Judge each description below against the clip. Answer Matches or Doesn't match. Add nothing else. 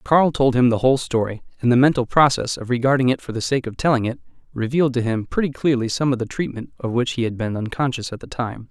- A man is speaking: Matches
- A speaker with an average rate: Doesn't match